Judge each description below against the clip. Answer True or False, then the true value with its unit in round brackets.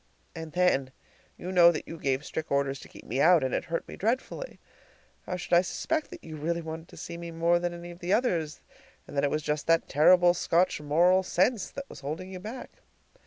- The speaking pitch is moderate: True (170 Hz)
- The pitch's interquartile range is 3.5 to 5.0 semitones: False (2.8 semitones)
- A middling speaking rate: False (225 wpm)